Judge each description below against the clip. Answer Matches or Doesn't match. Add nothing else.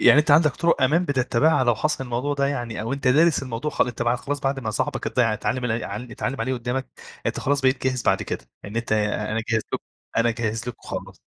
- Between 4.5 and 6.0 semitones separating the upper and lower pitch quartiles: Doesn't match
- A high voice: Doesn't match